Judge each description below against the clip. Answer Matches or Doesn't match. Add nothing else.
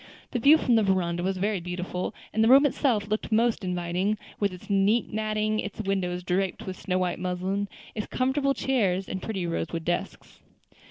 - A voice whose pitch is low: Doesn't match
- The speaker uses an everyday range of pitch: Matches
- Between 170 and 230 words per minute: Matches